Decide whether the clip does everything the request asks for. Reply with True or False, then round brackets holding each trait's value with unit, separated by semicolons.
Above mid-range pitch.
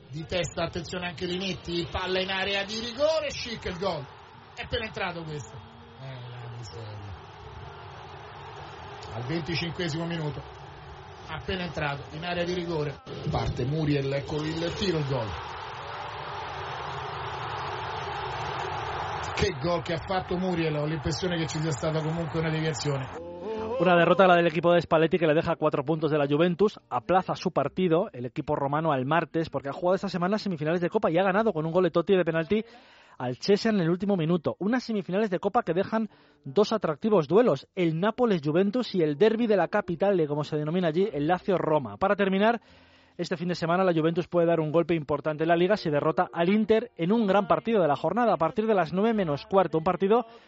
False (170 Hz)